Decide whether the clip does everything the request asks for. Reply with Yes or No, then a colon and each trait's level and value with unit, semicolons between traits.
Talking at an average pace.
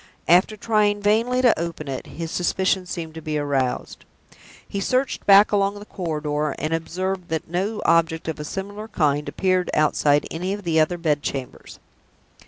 Yes: average, 170 wpm